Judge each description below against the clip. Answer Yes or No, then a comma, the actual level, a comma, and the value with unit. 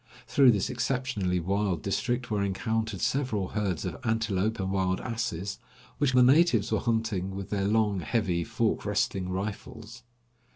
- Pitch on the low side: Yes, low, 105 Hz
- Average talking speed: Yes, average, 150 wpm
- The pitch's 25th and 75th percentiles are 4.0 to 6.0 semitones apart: No, average, 3.4 semitones